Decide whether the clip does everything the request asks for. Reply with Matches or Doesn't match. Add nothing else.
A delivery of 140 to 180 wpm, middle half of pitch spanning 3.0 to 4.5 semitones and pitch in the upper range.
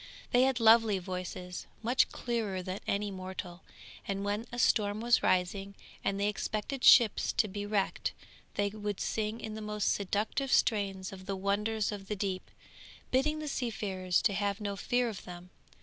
Doesn't match